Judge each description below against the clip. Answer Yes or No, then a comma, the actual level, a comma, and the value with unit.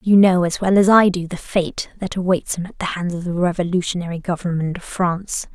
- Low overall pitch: No, medium, 180 Hz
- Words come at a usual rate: No, fast, 225 wpm